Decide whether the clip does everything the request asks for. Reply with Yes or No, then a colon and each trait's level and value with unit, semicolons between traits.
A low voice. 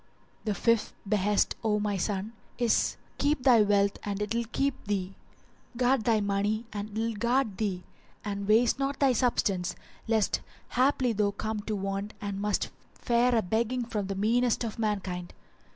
No: high, 215 Hz